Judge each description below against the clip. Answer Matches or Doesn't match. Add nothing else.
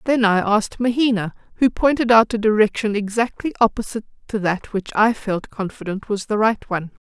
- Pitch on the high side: Matches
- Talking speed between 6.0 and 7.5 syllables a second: Doesn't match